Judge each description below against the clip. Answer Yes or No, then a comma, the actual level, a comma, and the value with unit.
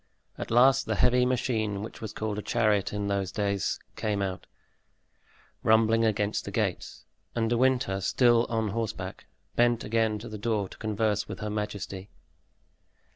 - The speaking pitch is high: No, low, 110 Hz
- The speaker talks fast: No, average, 160 wpm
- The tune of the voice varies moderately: No, narrow, 2.1 semitones